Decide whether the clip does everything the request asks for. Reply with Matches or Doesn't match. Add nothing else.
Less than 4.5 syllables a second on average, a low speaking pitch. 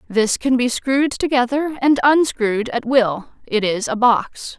Doesn't match